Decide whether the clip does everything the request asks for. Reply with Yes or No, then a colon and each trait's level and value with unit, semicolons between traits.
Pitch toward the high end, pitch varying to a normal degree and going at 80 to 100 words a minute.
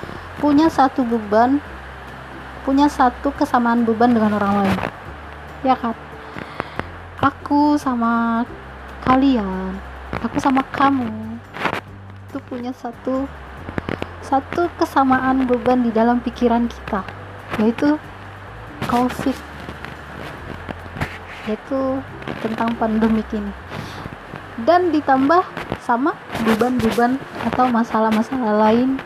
Yes: high, 245 Hz; average, 3.1 semitones; slow, 85 wpm